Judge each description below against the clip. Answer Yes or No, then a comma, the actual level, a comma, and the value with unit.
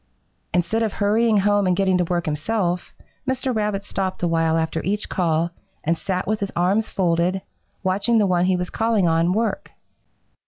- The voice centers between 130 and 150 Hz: No, medium, 185 Hz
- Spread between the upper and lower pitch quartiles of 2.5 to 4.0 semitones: Yes, average, 3.3 semitones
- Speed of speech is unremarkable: Yes, average, 180 wpm